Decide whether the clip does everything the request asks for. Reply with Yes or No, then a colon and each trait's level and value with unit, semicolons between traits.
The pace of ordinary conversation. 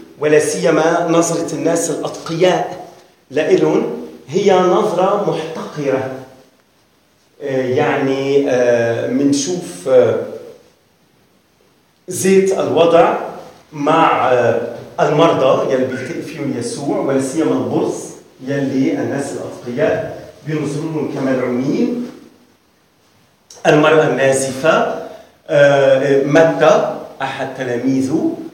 No: slow, 65 wpm